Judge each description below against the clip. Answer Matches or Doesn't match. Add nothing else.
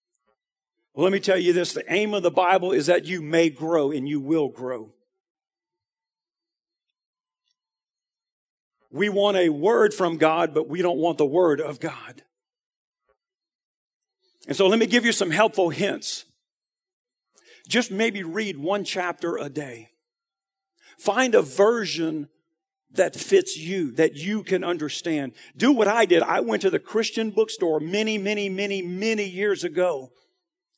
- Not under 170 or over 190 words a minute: Doesn't match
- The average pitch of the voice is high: Matches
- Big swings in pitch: Matches